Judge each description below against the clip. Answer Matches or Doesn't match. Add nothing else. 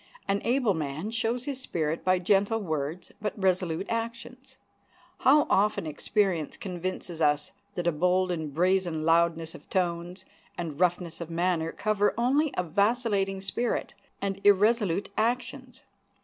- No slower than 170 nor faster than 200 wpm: Doesn't match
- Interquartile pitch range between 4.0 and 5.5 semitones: Matches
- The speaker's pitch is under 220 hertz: Matches